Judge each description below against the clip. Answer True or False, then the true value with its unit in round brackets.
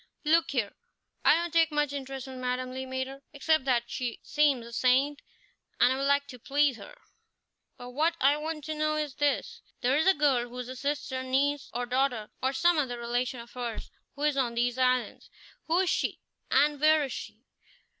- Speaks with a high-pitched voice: True (270 Hz)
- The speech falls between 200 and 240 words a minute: True (205 wpm)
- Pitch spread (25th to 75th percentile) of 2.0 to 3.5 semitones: True (2.9 semitones)